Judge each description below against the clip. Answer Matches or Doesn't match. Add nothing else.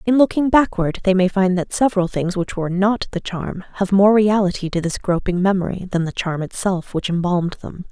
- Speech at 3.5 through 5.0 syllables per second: Doesn't match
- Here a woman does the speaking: Matches